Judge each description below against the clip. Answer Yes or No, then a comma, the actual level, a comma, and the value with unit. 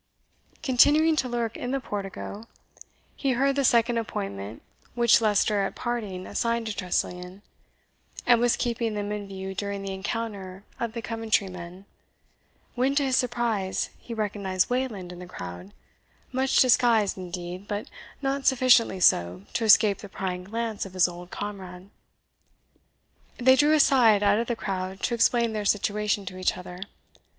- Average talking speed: Yes, average, 155 wpm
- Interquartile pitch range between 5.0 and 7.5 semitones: No, average, 4.1 semitones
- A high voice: Yes, high, 210 Hz